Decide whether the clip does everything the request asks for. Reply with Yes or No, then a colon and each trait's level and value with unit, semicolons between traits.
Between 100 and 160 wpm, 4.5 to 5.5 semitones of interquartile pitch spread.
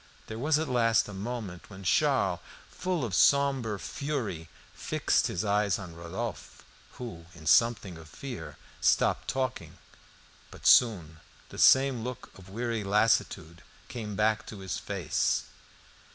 Yes: average, 140 wpm; average, 4.8 semitones